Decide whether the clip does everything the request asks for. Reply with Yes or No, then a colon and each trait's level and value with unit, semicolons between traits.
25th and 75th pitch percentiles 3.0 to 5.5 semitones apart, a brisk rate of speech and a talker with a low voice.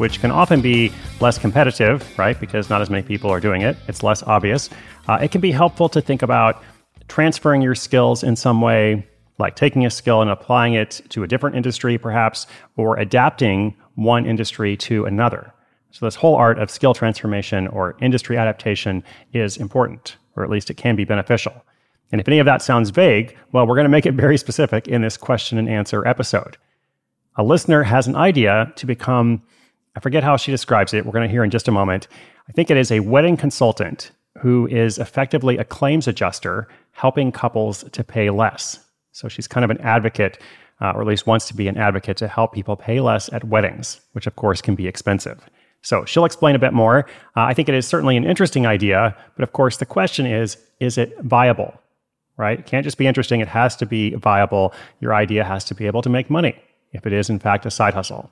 Yes: average, 3.5 semitones; fast, 215 wpm; low, 115 Hz